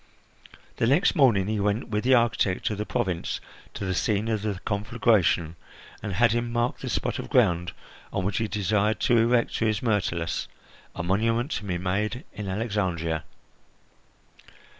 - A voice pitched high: No, low, 105 Hz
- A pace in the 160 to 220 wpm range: Yes, average, 165 wpm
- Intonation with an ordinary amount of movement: Yes, average, 3.5 semitones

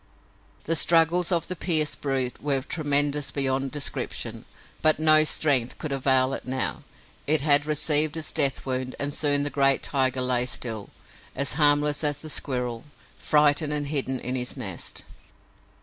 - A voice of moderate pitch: Yes, medium, 145 Hz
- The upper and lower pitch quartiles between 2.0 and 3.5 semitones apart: Yes, narrow, 2.5 semitones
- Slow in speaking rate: No, average, 155 wpm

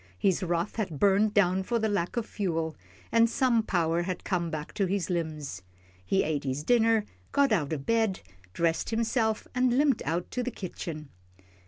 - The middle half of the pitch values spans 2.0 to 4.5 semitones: No, wide, 5.4 semitones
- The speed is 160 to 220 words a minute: Yes, average, 175 wpm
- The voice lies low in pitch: No, high, 190 Hz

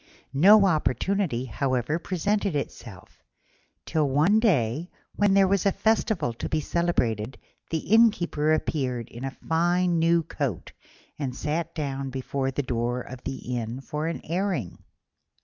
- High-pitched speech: No, medium, 150 Hz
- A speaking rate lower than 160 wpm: Yes, average, 140 wpm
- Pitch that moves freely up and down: Yes, wide, 5.7 semitones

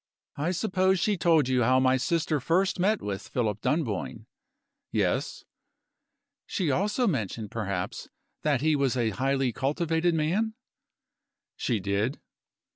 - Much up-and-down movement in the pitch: Yes, wide, 6.5 semitones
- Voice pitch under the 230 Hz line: Yes, medium, 140 Hz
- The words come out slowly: Yes, slow, 125 wpm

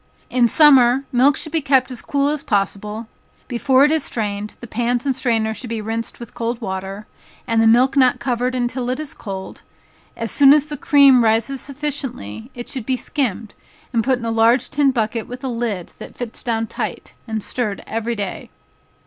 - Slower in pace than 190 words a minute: No, average, 195 wpm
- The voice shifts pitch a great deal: No, average, 3.2 semitones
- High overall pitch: Yes, high, 240 Hz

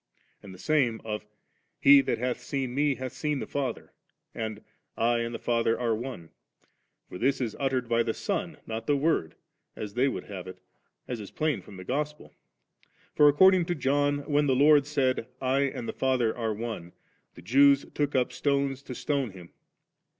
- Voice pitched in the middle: No, low, 130 Hz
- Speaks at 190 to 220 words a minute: Yes, average, 195 wpm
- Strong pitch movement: No, average, 3.8 semitones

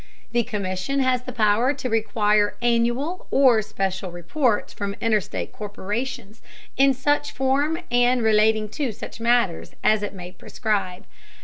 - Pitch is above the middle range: Yes, high, 225 Hz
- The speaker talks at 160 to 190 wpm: No, slow, 135 wpm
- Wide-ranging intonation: No, average, 3.7 semitones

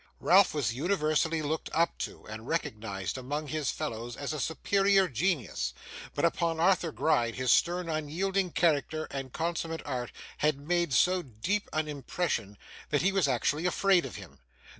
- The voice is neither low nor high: Yes, medium, 155 Hz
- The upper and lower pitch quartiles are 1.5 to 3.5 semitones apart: No, average, 5.0 semitones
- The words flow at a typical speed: Yes, average, 160 wpm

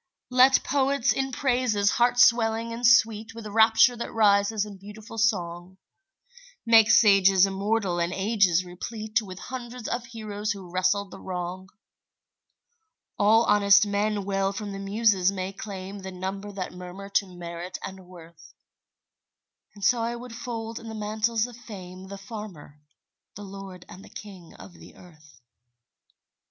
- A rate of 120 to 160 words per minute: Yes, average, 150 wpm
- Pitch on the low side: No, high, 205 Hz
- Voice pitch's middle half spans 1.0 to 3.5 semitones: Yes, average, 3.2 semitones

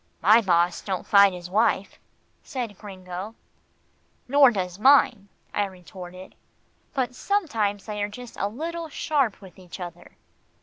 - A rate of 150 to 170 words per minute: No, slow, 135 wpm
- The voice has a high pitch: Yes, high, 205 Hz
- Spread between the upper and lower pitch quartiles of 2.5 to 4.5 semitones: No, average, 5.0 semitones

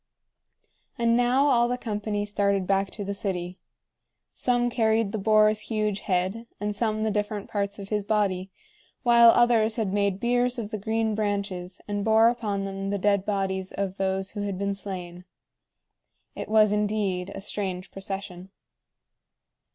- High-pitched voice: Yes, high, 205 Hz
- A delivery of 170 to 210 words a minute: No, average, 160 wpm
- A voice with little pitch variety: Yes, narrow, 2.1 semitones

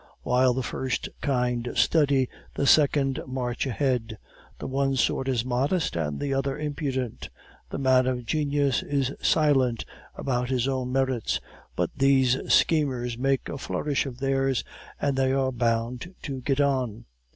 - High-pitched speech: No, low, 130 Hz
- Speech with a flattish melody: Yes, narrow, 1.9 semitones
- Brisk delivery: No, average, 150 wpm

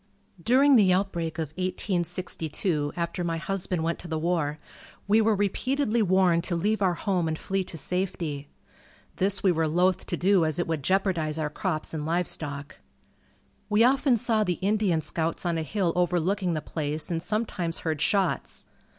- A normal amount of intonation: Yes, average, 3.4 semitones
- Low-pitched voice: No, medium, 175 Hz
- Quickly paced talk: No, average, 170 wpm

